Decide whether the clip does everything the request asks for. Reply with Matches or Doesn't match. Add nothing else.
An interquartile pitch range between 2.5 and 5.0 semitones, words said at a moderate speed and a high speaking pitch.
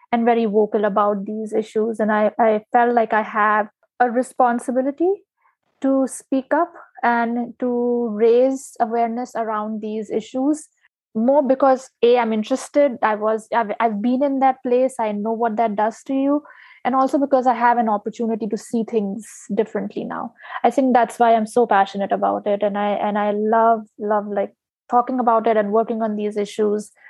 Matches